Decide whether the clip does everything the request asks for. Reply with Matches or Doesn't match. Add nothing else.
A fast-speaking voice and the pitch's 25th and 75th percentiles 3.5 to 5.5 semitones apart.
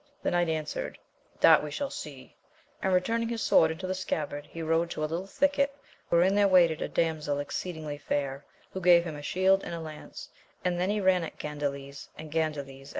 Matches